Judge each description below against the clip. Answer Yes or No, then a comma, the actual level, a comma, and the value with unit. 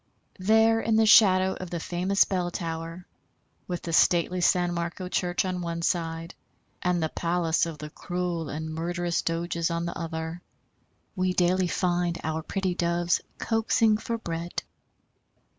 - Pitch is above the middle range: No, medium, 175 Hz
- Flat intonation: Yes, narrow, 1.7 semitones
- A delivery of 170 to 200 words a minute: No, average, 150 wpm